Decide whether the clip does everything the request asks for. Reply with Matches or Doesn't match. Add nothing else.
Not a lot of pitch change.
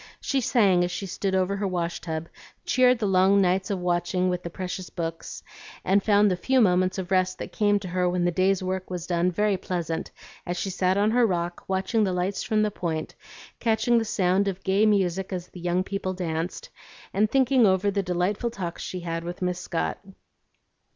Matches